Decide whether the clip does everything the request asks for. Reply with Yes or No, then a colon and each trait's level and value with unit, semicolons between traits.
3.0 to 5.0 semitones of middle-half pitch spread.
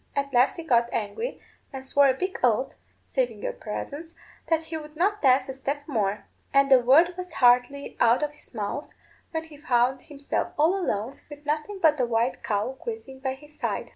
Yes: average, 4.2 semitones